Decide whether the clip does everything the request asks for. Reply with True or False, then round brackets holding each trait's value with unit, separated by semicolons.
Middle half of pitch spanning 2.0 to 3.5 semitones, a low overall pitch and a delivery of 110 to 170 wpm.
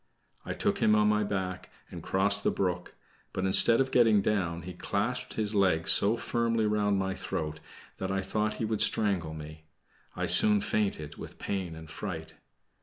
False (3.1 semitones; 100 Hz; 180 wpm)